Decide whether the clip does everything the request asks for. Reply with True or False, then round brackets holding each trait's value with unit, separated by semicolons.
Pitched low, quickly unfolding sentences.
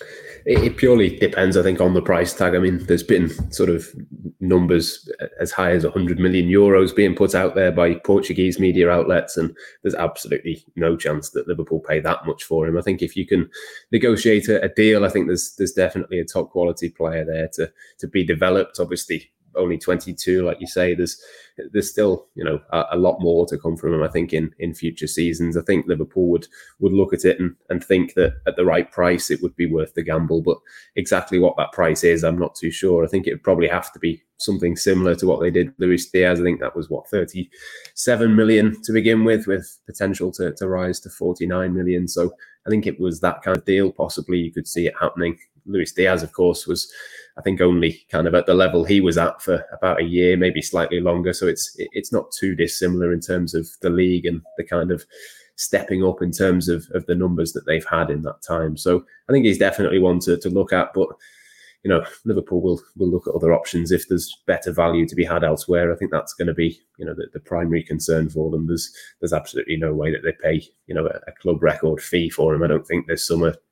True (90 Hz; 235 wpm)